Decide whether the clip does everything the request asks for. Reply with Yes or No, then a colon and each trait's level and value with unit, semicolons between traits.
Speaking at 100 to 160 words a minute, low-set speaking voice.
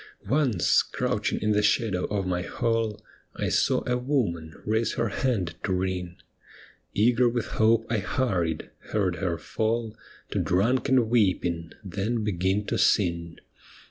Yes: average, 140 wpm; low, 105 Hz